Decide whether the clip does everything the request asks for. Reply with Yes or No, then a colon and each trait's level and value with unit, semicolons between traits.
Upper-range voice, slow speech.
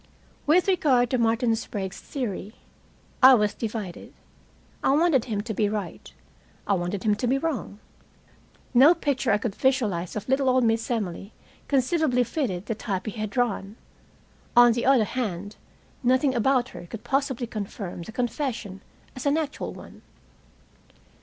No: high, 235 Hz; average, 155 wpm